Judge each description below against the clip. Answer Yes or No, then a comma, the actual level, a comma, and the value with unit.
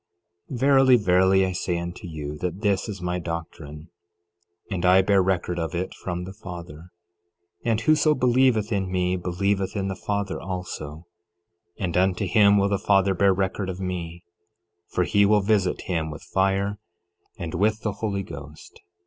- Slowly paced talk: No, average, 165 wpm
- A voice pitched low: Yes, very low, 95 Hz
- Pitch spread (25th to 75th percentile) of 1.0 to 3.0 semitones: Yes, narrow, 2.4 semitones